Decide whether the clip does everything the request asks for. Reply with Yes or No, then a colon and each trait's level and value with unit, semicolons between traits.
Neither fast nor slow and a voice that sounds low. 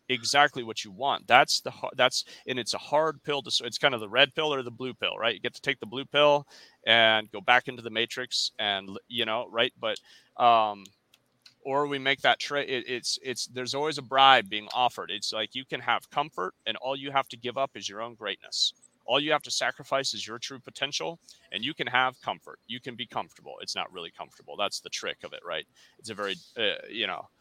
No: fast, 240 wpm; low, 130 Hz